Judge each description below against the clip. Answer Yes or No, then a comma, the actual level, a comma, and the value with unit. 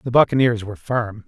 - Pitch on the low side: Yes, low, 115 Hz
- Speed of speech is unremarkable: Yes, average, 190 wpm